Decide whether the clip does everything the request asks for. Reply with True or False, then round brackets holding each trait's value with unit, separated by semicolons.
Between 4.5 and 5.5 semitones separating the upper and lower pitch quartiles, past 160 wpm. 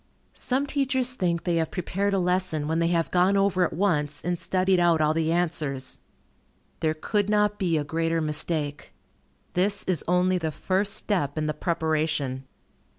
False (3.3 semitones; 170 wpm)